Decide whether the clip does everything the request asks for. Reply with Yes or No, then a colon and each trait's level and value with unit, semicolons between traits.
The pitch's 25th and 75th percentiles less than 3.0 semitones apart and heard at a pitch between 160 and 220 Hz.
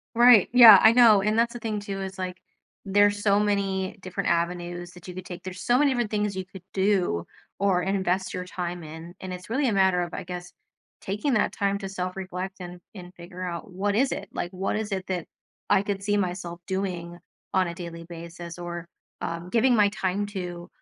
Yes: narrow, 2.5 semitones; high, 190 Hz